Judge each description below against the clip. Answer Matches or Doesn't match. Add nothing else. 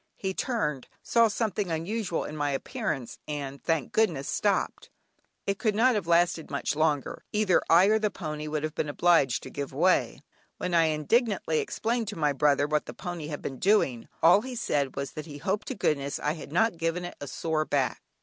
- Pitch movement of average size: Doesn't match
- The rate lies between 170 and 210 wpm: Matches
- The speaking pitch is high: Doesn't match